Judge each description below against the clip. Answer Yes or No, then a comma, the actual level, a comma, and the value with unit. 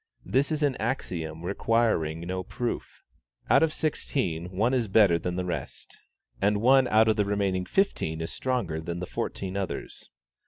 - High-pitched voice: No, low, 100 Hz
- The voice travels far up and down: Yes, wide, 5.8 semitones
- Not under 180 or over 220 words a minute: No, average, 165 wpm